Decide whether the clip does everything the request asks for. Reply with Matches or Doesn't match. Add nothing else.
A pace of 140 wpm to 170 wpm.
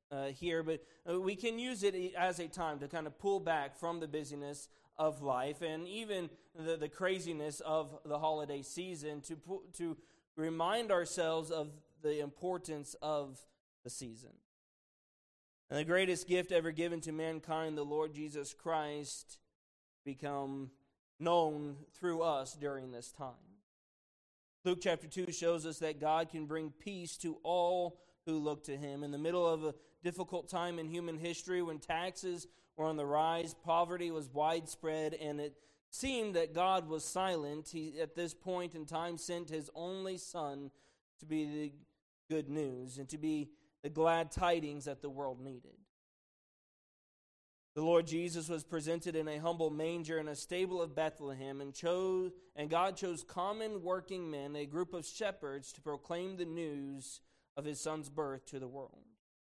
Matches